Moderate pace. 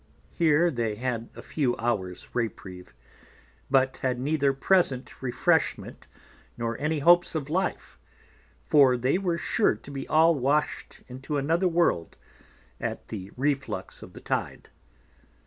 No: slow, 130 wpm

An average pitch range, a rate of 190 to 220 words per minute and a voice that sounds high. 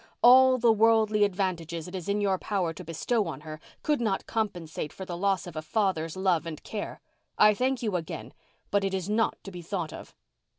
Yes: average, 4.1 semitones; fast, 205 wpm; high, 195 Hz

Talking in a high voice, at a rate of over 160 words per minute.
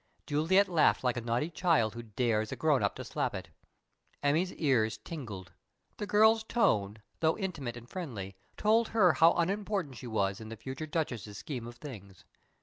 No: low, 135 Hz; average, 175 wpm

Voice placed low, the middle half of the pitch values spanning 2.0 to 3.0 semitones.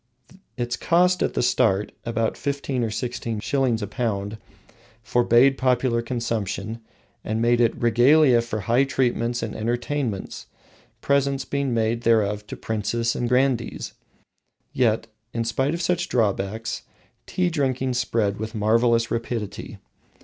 Yes: low, 120 Hz; average, 2.7 semitones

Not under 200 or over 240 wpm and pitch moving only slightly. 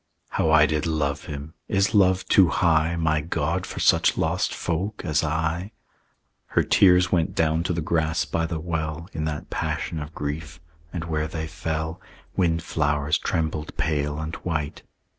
No: average, 160 wpm; narrow, 1.6 semitones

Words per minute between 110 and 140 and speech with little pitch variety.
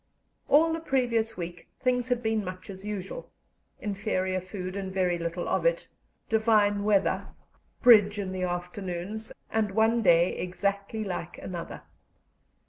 No: slow, 135 wpm; average, 3.3 semitones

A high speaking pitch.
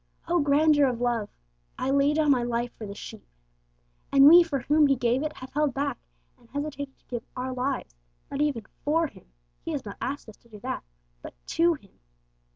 Yes: very high, 275 Hz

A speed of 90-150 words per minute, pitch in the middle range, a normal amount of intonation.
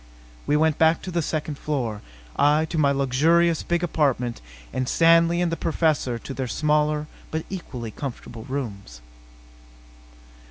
Yes: average, 145 wpm; medium, 150 Hz; average, 4.2 semitones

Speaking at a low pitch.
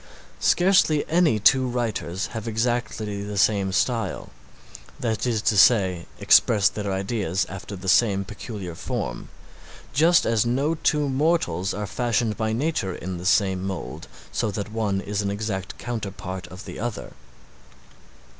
Yes: low, 105 Hz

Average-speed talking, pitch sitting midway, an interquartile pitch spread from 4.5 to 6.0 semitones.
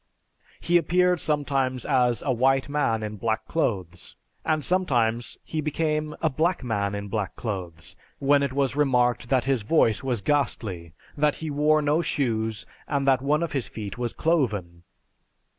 No: average, 160 wpm; low, 130 Hz; average, 5.1 semitones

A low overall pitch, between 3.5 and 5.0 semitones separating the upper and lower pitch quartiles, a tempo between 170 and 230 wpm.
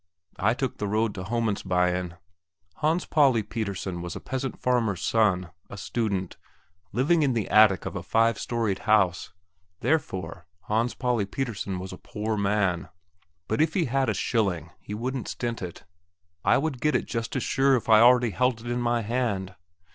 Yes: low, 110 Hz; average, 4.4 semitones; average, 175 wpm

